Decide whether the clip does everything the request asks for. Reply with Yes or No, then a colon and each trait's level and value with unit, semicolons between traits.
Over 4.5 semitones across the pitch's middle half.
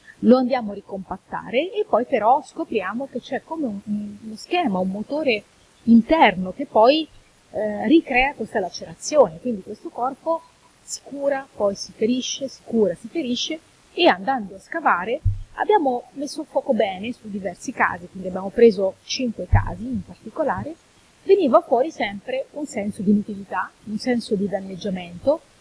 Yes: wide, 5.4 semitones